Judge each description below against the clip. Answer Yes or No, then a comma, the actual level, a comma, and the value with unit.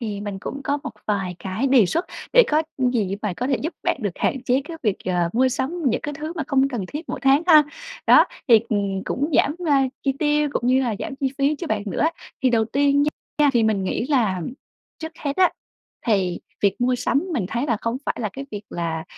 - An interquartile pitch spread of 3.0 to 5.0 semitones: No, wide, 5.6 semitones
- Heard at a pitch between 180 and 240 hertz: No, very high, 255 Hz